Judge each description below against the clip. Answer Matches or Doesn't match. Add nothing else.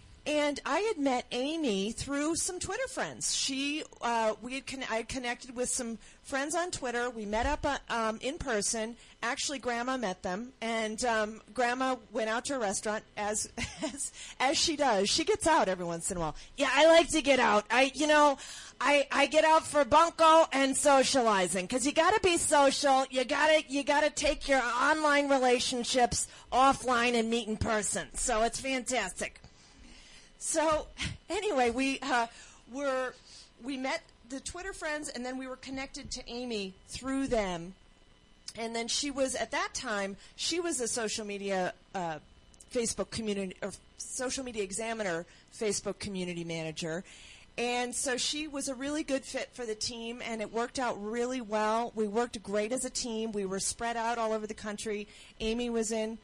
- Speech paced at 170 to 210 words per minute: Matches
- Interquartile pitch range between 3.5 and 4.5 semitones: Matches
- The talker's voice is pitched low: Doesn't match